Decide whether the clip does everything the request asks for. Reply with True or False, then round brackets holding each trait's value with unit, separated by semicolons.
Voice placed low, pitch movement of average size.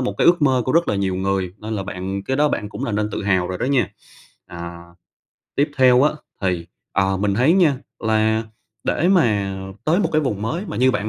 False (110 Hz; 5.7 semitones)